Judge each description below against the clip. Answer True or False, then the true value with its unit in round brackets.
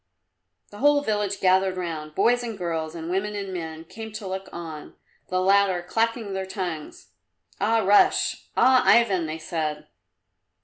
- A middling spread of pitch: True (4.0 semitones)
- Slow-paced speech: False (150 wpm)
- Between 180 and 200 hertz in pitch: True (190 Hz)